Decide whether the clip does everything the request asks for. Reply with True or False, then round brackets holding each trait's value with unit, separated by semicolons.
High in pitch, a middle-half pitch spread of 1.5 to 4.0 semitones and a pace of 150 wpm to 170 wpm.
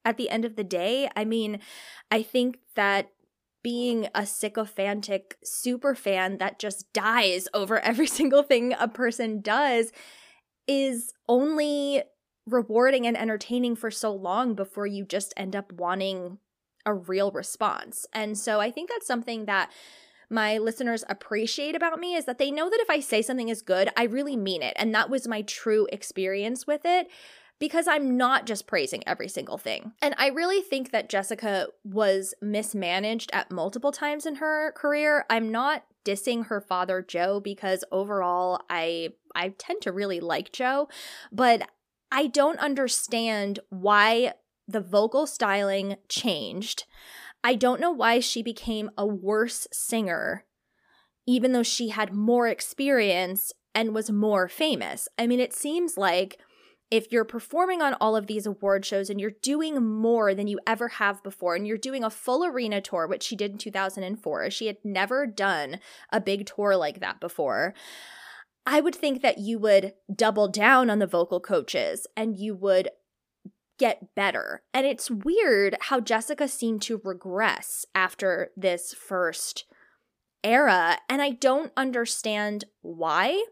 False (225 Hz; 4.6 semitones; 160 wpm)